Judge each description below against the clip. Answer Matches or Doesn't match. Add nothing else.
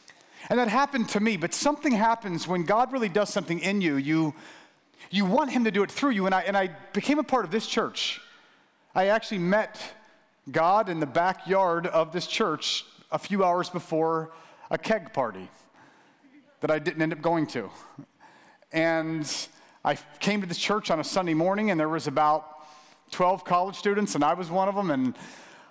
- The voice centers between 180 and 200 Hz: Matches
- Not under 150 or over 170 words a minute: Doesn't match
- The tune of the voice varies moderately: Matches